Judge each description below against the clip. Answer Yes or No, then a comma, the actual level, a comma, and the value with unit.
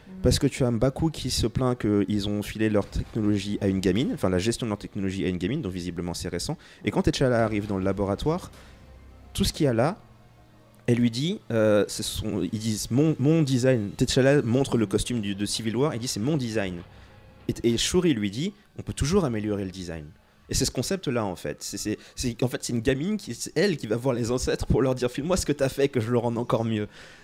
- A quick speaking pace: Yes, fast, 250 wpm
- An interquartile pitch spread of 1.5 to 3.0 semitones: No, average, 4.5 semitones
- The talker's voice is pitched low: Yes, low, 115 Hz